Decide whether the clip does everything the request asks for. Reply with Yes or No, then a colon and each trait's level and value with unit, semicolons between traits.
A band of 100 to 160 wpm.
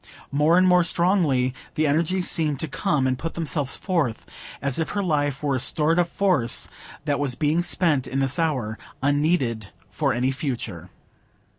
No: average, 170 wpm